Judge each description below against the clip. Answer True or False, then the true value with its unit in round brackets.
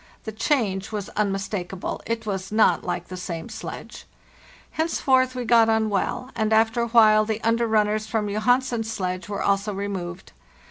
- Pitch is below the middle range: False (215 Hz)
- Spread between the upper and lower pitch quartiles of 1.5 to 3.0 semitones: True (2.5 semitones)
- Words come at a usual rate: True (170 wpm)